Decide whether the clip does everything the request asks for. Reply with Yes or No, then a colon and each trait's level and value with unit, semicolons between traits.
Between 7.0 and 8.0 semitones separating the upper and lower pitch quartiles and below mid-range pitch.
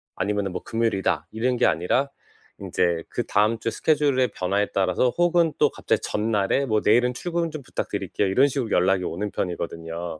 No: wide, 5.5 semitones; low, 110 Hz